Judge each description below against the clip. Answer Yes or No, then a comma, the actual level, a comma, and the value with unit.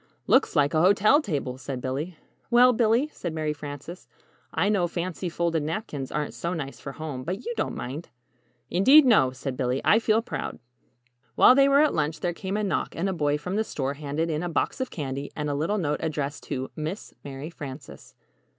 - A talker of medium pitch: Yes, medium, 160 Hz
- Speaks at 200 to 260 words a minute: Yes, fast, 205 wpm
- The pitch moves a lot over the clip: Yes, wide, 5.7 semitones